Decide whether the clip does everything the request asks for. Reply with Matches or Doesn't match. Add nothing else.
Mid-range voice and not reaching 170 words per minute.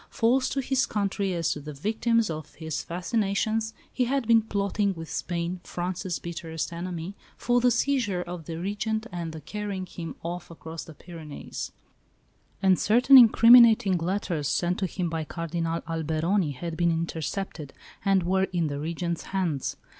Matches